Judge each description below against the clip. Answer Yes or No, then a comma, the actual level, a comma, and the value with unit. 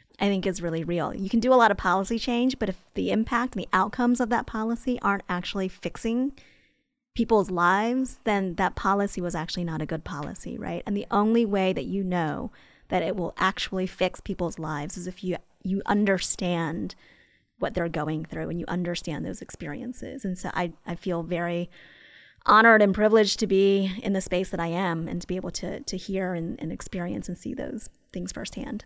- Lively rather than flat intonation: No, average, 3.9 semitones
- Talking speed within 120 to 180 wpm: No, fast, 205 wpm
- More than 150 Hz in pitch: Yes, high, 190 Hz